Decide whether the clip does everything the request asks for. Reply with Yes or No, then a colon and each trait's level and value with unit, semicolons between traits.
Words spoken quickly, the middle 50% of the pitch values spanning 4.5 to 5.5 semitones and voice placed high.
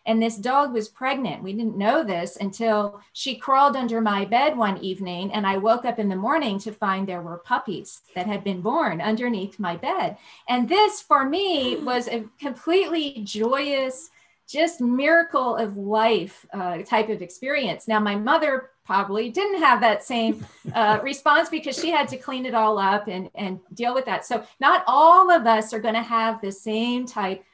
No: average, 190 wpm; average, 4.9 semitones; high, 225 Hz